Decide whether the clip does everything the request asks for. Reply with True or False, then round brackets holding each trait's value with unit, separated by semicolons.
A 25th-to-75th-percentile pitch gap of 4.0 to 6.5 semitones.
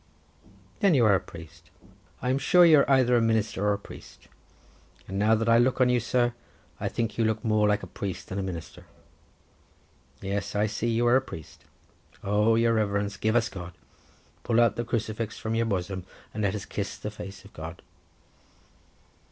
False (2.8 semitones)